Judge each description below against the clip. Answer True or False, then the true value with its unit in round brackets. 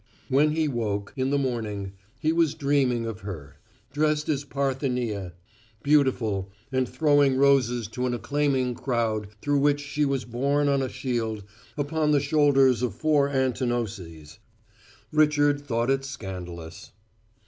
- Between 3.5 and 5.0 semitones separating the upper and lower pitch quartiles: True (4.1 semitones)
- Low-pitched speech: True (130 Hz)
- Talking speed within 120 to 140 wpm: True (135 wpm)